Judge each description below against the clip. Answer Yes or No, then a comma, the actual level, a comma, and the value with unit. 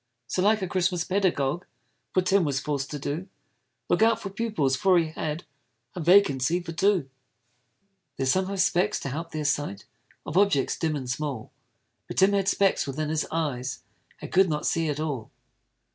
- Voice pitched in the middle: Yes, medium, 165 Hz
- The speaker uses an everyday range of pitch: Yes, average, 4.8 semitones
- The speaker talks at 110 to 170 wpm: No, average, 180 wpm